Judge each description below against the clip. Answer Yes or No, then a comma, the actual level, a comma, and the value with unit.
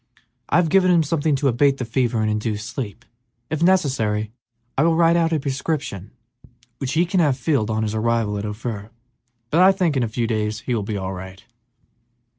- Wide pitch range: Yes, wide, 6.8 semitones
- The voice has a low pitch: Yes, low, 125 Hz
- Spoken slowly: No, fast, 205 wpm